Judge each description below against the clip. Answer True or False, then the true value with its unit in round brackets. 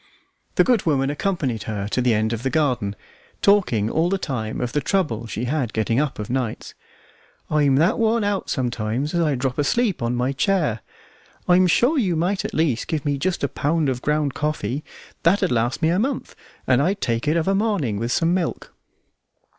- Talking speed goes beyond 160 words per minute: True (200 wpm)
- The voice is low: False (145 Hz)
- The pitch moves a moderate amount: False (6.5 semitones)